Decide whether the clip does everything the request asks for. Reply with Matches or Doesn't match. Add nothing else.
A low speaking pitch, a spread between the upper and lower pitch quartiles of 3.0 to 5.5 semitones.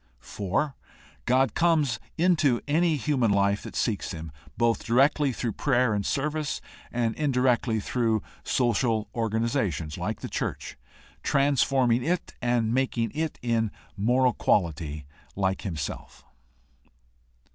Matches